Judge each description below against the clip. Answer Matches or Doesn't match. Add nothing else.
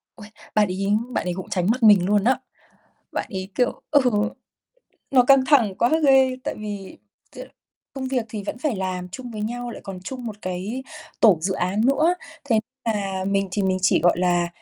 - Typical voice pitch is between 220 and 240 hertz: Doesn't match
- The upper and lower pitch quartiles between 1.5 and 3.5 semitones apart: Doesn't match